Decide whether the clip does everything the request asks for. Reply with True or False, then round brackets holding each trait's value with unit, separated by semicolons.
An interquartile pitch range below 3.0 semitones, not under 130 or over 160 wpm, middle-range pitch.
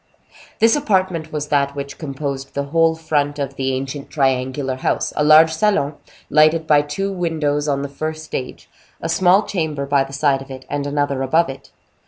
False (2.6 semitones; 185 wpm; 145 Hz)